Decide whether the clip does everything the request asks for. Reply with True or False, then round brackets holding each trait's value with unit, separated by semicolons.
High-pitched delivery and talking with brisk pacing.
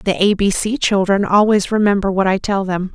True (195 Hz; 225 wpm)